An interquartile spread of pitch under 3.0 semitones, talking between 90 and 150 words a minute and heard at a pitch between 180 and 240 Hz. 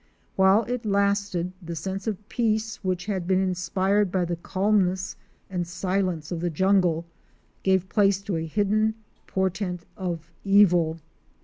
Yes: narrow, 2.4 semitones; average, 140 wpm; high, 190 Hz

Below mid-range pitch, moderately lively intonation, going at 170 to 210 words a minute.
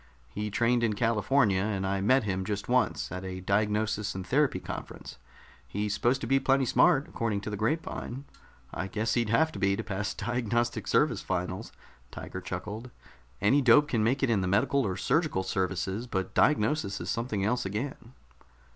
Yes: low, 110 Hz; average, 4.2 semitones; average, 180 wpm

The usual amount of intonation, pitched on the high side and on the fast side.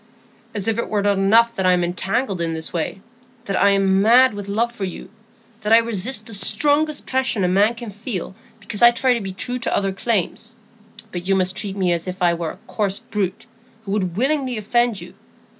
Yes: average, 3.7 semitones; high, 205 Hz; fast, 210 wpm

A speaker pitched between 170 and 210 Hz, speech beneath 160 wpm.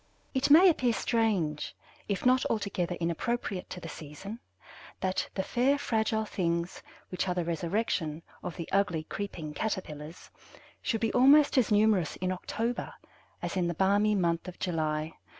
Yes: high, 190 Hz; average, 150 wpm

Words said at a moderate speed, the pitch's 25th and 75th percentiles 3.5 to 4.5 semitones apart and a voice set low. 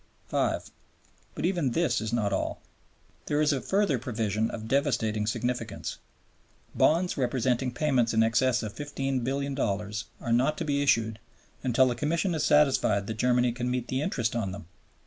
Yes: average, 160 wpm; average, 4.0 semitones; low, 125 Hz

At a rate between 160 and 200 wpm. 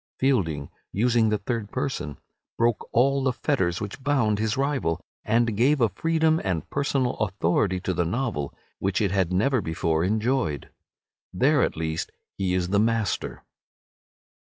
No: average, 150 wpm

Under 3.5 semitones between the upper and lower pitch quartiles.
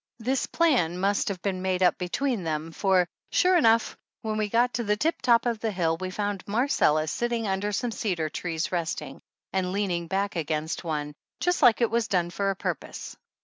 No: average, 4.9 semitones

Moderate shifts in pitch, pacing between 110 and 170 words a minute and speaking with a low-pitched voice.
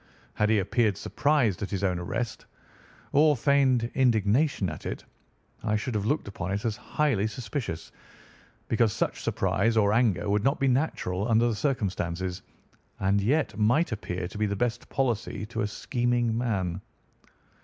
Yes: average, 3.6 semitones; average, 160 wpm; low, 110 Hz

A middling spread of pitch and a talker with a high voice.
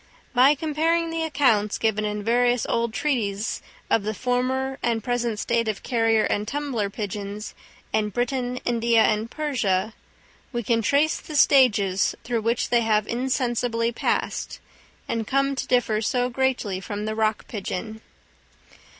Yes: average, 3.2 semitones; high, 235 Hz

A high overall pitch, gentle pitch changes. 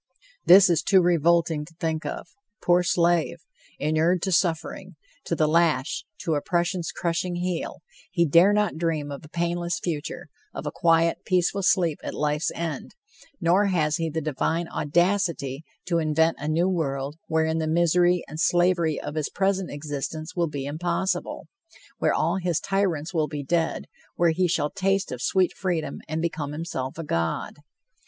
No: medium, 165 Hz; narrow, 2.3 semitones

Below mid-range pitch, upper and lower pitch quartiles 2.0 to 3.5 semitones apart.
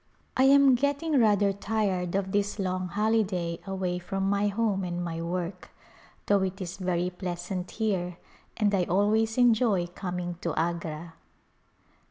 No: high, 190 Hz; average, 3.0 semitones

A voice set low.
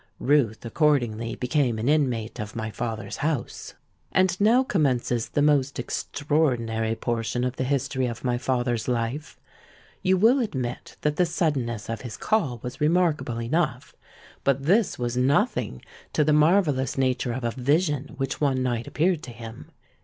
Yes: low, 130 Hz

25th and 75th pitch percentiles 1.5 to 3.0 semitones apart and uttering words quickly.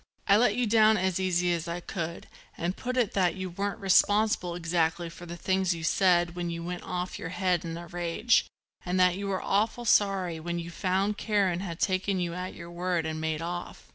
Yes: narrow, 2.4 semitones; fast, 215 wpm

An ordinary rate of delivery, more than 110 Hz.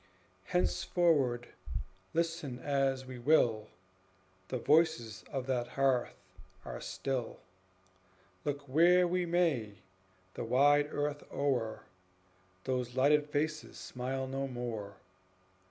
No: slow, 100 wpm; low, 135 Hz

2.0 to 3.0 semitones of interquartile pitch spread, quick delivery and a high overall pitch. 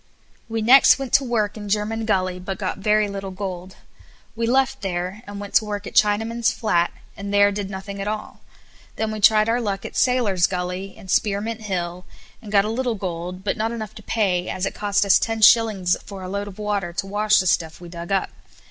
Yes: narrow, 2.5 semitones; fast, 215 wpm; high, 205 Hz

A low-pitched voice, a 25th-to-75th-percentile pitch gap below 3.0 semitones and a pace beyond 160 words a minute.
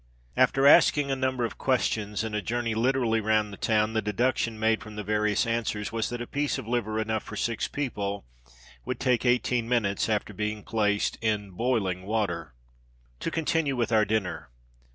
Yes: low, 110 Hz; narrow, 2.4 semitones; average, 180 wpm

